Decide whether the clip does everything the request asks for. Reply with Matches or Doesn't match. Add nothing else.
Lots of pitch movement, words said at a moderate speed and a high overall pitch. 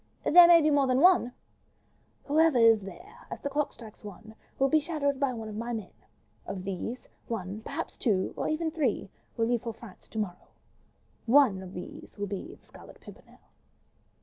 Matches